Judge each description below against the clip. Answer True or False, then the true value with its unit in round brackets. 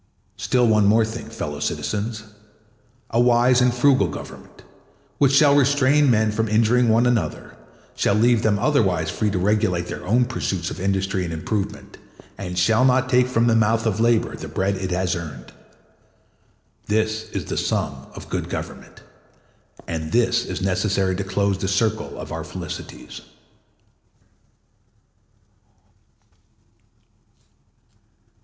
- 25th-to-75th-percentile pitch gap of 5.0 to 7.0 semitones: False (3.8 semitones)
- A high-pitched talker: False (110 Hz)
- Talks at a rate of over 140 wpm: False (135 wpm)